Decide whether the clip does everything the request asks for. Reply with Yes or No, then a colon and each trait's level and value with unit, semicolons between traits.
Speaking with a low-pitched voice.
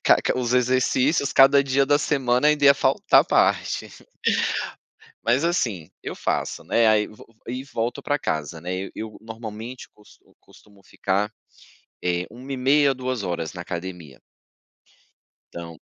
Yes: low, 120 Hz